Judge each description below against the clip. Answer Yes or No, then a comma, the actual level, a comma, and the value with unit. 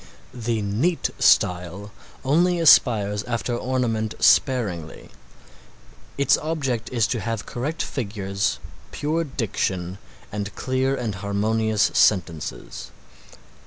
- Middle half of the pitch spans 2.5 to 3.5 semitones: No, average, 4.4 semitones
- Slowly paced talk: Yes, slow, 95 wpm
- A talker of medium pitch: No, low, 115 Hz